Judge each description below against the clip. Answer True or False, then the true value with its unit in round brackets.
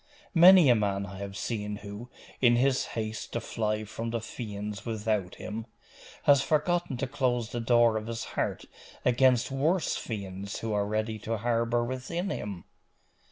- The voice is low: True (115 Hz)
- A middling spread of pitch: True (3.3 semitones)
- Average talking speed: True (160 wpm)